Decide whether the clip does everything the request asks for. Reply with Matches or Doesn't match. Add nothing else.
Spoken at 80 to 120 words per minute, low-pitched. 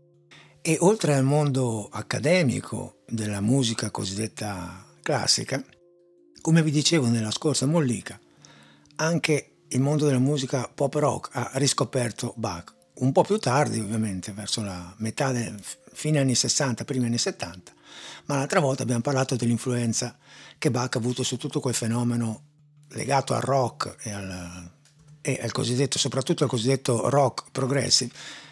Doesn't match